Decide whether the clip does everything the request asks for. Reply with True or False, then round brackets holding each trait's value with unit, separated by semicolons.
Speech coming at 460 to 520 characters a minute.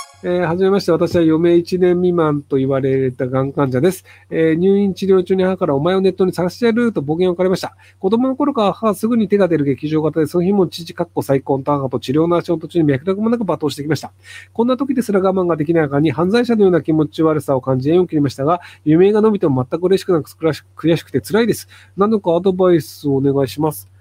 True (470 characters per minute)